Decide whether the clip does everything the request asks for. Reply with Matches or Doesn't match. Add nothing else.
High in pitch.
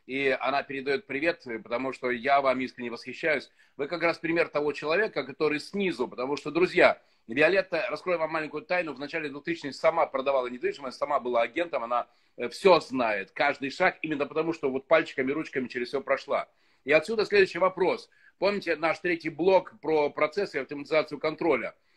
Doesn't match